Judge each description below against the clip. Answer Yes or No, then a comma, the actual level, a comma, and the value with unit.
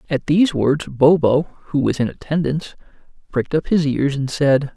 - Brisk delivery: No, average, 175 wpm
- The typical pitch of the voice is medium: Yes, medium, 145 Hz